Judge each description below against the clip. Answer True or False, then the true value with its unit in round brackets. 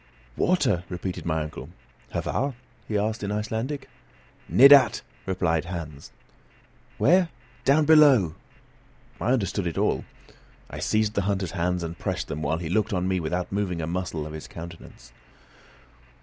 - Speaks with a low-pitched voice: True (95 Hz)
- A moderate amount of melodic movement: True (4.9 semitones)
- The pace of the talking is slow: False (145 wpm)